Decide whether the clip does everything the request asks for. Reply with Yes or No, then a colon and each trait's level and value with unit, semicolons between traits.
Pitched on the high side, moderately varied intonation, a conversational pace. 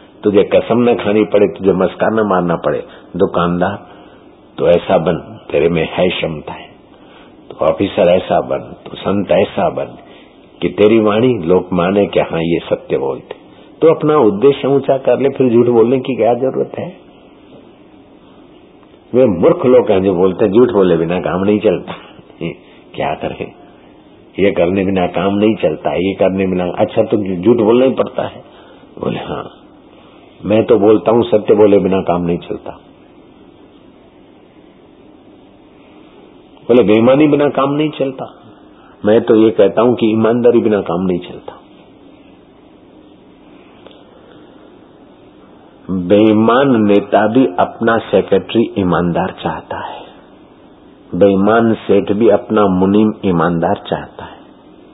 No: low, 105 Hz; average, 4.2 semitones; average, 135 wpm